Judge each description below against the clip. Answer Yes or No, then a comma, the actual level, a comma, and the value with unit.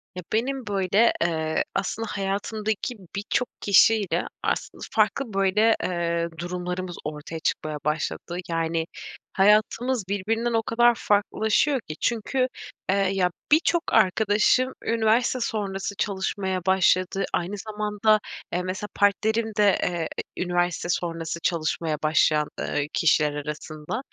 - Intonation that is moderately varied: Yes, average, 4.1 semitones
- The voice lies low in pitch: No, high, 195 Hz